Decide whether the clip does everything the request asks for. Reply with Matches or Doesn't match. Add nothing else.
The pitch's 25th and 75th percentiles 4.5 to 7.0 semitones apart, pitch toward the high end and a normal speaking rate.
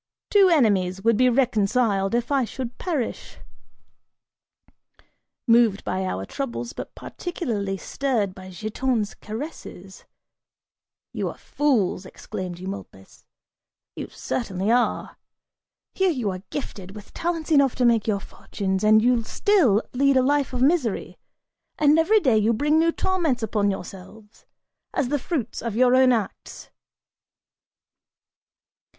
Doesn't match